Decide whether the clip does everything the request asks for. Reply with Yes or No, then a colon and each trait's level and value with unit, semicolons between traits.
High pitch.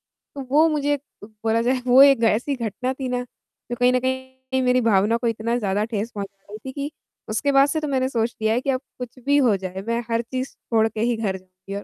Yes: high, 240 Hz